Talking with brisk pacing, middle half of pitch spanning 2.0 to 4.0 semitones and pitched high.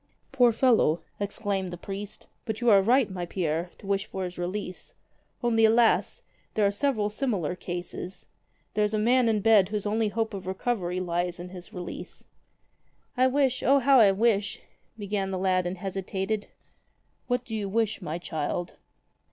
No: average, 175 wpm; average, 3.6 semitones; high, 205 Hz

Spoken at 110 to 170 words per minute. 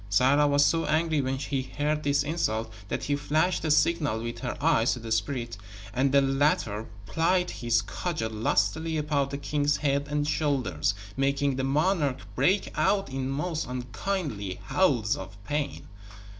Yes: average, 160 wpm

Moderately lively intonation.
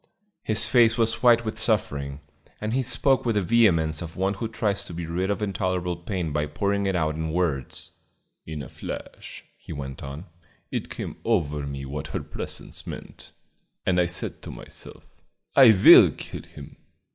No: wide, 5.8 semitones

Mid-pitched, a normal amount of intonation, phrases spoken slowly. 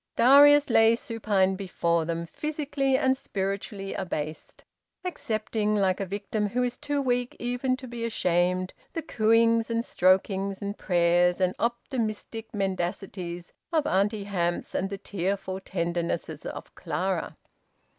No: high, 200 Hz; average, 4.3 semitones; slow, 130 wpm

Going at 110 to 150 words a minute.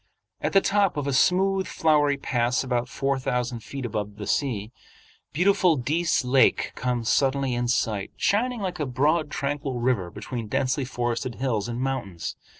No: average, 160 wpm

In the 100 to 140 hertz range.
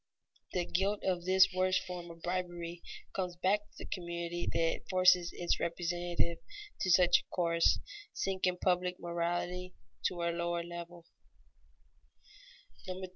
No: medium, 175 Hz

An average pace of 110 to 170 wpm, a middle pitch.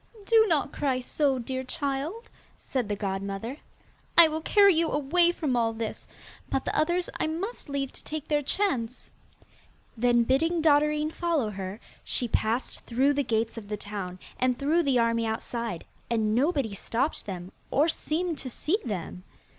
No: average, 165 wpm; very high, 265 Hz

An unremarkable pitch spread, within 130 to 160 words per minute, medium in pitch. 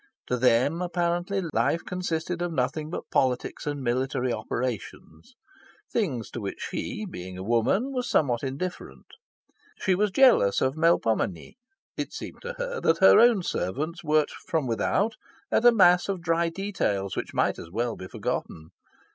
No: wide, 7.4 semitones; average, 155 wpm; medium, 160 Hz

